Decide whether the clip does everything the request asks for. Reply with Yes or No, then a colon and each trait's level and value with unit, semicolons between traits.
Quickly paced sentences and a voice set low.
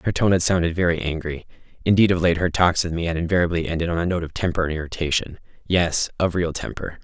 Yes: fast, 220 wpm; very low, 85 Hz